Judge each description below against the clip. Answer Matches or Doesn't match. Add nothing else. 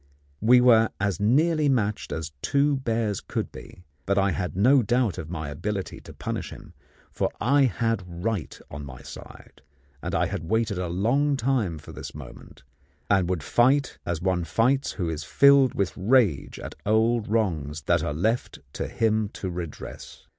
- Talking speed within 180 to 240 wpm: Doesn't match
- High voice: Doesn't match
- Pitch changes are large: Matches